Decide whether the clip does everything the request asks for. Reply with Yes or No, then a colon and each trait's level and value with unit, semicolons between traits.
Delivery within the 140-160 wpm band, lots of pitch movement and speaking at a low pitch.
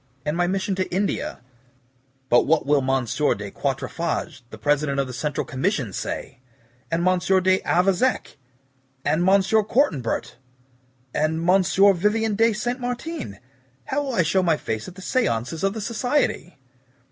No: average, 155 wpm; wide, 6.1 semitones; medium, 180 Hz